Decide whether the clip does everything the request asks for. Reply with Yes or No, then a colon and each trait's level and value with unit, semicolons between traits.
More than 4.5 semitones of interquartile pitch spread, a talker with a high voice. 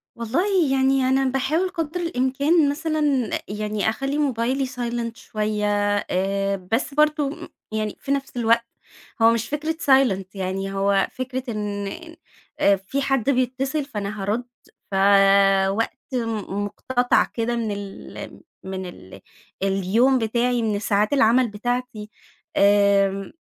Yes: average, 5.0 semitones; high, 230 Hz